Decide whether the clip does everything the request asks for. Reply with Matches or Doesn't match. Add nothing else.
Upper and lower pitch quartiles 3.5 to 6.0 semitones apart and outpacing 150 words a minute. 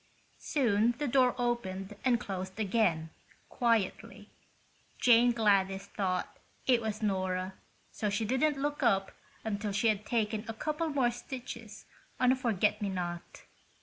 Doesn't match